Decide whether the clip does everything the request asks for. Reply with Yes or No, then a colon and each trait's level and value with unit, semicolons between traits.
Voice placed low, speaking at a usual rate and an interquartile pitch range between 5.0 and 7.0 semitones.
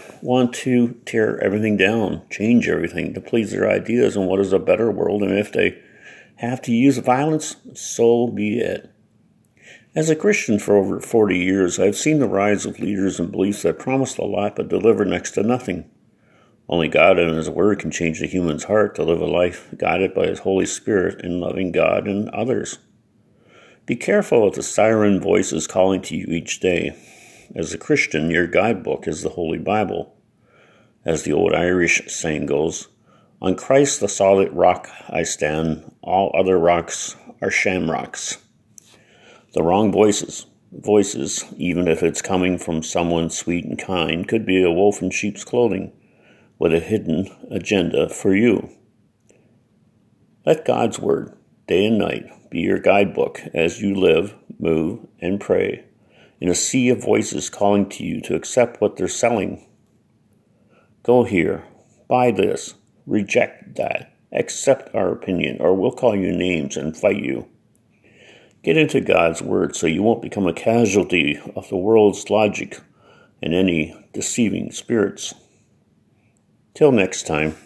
No: very low, 95 Hz; average, 160 wpm; average, 4.4 semitones